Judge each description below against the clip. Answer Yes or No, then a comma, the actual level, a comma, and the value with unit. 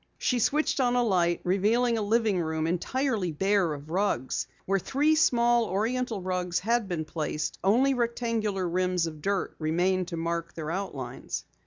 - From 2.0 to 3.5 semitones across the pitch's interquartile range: No, wide, 5.6 semitones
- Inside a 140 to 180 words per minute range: Yes, average, 160 wpm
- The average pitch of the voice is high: Yes, high, 195 Hz